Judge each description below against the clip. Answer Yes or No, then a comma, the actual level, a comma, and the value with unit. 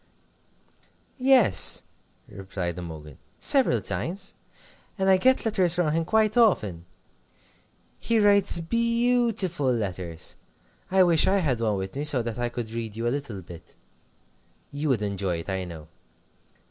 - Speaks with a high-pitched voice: No, medium, 140 Hz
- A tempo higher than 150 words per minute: No, average, 140 wpm